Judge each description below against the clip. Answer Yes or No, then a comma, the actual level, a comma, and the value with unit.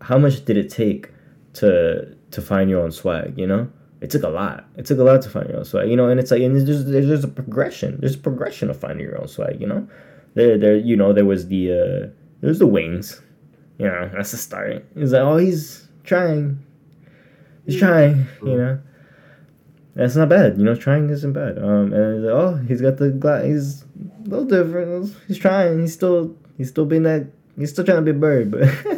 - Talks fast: Yes, fast, 225 wpm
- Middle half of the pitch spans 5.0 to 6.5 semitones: Yes, wide, 5.4 semitones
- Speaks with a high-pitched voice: No, medium, 140 Hz